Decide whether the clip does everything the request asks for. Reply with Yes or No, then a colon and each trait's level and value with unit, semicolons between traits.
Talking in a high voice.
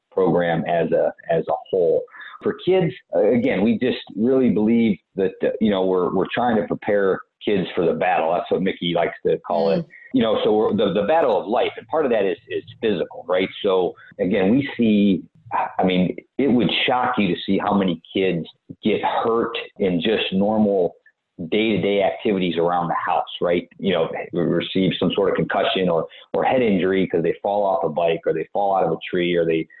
No: low, 105 Hz